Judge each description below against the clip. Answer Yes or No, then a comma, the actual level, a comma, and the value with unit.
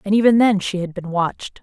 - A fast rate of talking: Yes, fast, 260 wpm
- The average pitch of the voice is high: Yes, high, 195 Hz